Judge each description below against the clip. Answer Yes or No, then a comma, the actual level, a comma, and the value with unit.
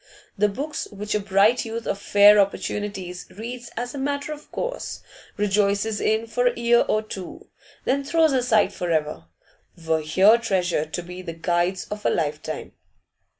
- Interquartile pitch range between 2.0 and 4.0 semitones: No, average, 4.5 semitones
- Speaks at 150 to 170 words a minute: Yes, average, 165 wpm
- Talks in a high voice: Yes, high, 210 Hz